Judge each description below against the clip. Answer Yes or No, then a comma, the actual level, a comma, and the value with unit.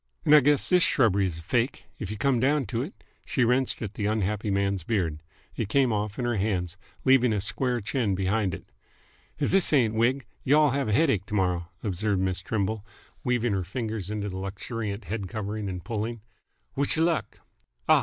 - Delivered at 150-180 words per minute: No, average, 200 wpm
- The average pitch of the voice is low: Yes, low, 110 Hz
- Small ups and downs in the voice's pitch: No, average, 4.2 semitones